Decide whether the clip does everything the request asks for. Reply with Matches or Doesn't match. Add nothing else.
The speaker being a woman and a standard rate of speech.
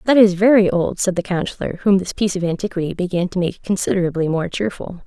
Doesn't match